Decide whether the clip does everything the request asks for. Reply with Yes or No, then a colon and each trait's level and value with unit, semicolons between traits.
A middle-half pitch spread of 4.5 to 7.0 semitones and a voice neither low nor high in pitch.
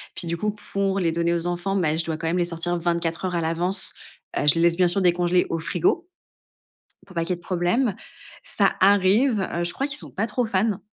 No: narrow, 2.6 semitones; medium, 175 Hz